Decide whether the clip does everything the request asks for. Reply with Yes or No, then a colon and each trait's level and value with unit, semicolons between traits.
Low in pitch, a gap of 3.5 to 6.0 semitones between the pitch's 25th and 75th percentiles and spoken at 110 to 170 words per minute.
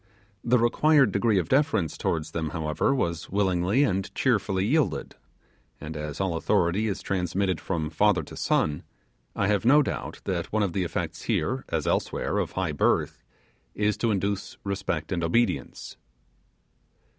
Yes: very low, 95 Hz; average, 4.5 semitones; average, 155 wpm